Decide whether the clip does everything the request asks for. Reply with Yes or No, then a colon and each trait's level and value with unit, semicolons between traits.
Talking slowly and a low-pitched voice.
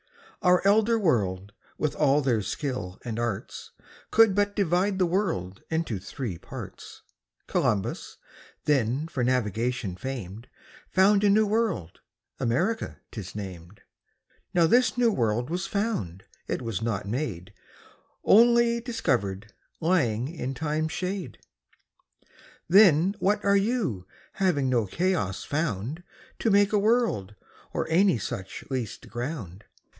No: slow, 125 wpm; medium, 145 Hz